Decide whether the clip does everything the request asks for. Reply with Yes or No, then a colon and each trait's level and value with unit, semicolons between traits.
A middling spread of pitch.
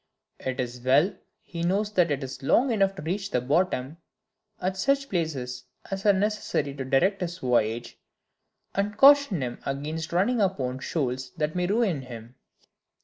No: wide, 7.0 semitones